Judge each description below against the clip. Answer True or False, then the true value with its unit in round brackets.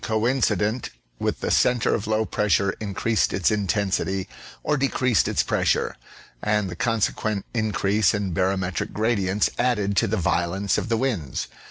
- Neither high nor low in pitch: False (105 Hz)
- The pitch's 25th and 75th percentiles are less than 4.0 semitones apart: True (2.7 semitones)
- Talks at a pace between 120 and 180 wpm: True (150 wpm)